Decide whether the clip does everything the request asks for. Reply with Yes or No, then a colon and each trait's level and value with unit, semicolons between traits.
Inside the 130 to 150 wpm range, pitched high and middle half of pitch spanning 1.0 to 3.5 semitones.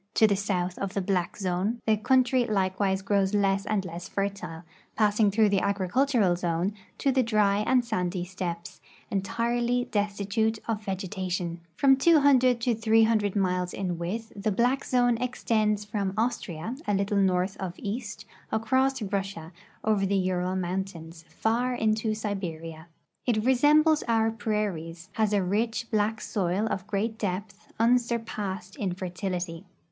Yes: average, 145 wpm; high, 205 Hz; average, 3.2 semitones